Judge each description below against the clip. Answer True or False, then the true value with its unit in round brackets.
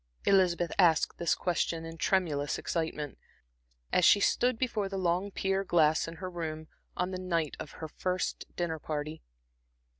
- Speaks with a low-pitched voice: False (170 Hz)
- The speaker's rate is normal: True (155 wpm)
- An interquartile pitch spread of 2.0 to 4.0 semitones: True (2.8 semitones)